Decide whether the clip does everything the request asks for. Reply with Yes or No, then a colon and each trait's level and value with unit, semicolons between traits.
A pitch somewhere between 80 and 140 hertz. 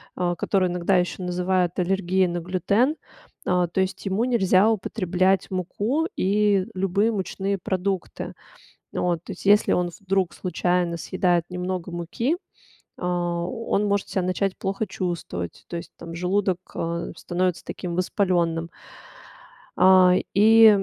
No: medium, 185 Hz